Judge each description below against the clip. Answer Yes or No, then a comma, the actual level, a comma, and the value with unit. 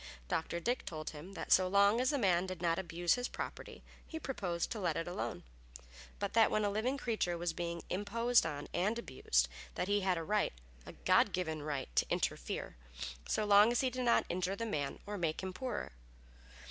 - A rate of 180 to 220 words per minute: Yes, fast, 205 wpm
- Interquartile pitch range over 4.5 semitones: Yes, average, 4.9 semitones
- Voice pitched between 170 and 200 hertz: Yes, high, 190 Hz